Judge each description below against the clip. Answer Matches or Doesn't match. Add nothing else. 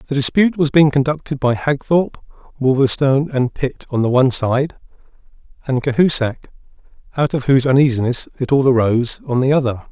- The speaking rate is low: Doesn't match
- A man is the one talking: Matches